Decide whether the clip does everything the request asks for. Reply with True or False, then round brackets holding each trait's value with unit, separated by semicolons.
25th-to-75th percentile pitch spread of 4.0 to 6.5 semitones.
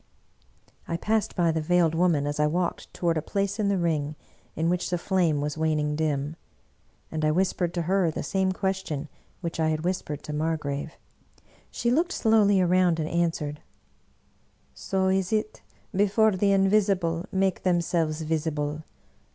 False (3.5 semitones)